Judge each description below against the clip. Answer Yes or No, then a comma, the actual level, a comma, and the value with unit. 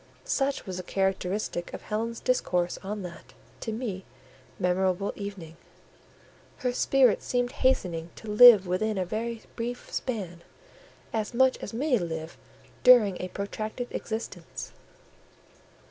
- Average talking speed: No, slow, 125 wpm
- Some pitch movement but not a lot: Yes, average, 4.9 semitones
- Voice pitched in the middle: No, high, 210 Hz